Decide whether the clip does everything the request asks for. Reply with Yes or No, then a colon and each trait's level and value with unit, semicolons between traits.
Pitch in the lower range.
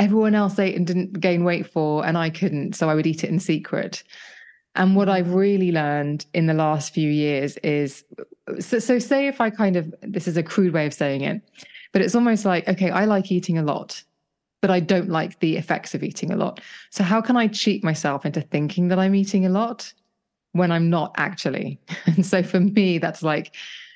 No: medium, 180 Hz